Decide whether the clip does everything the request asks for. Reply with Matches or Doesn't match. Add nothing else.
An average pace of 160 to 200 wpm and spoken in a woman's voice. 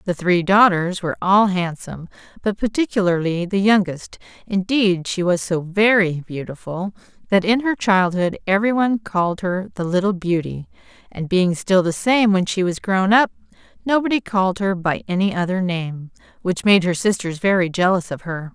Matches